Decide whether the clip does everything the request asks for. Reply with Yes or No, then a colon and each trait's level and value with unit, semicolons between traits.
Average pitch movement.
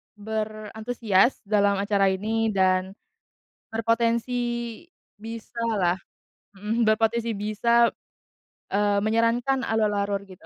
No: narrow, 2.3 semitones